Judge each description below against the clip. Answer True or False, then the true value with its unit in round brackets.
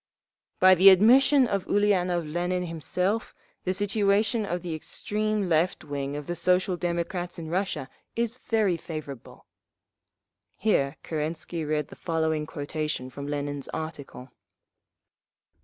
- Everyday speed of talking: False (125 wpm)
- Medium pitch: True (175 Hz)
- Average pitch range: True (4.3 semitones)